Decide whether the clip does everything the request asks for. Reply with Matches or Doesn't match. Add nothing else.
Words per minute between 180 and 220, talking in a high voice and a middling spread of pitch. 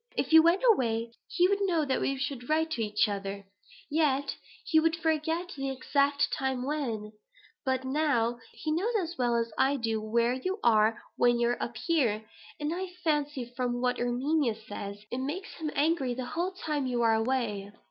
Matches